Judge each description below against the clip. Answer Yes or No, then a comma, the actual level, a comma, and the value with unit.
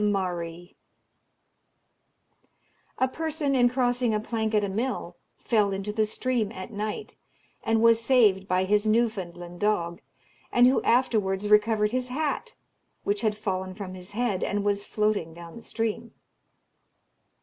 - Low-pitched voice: No, high, 215 Hz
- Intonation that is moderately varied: Yes, average, 3.4 semitones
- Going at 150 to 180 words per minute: No, average, 140 wpm